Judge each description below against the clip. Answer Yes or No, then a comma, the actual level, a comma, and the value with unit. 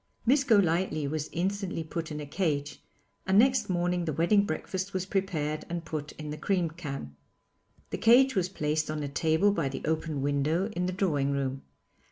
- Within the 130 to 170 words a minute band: No, average, 185 wpm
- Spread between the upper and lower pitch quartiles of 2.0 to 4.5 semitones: Yes, average, 4.2 semitones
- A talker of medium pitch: Yes, medium, 165 Hz